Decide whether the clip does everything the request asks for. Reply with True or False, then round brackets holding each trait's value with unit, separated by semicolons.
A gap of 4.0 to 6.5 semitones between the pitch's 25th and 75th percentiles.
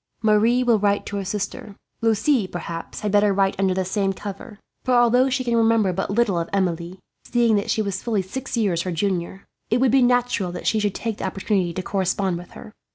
False (3.5 semitones)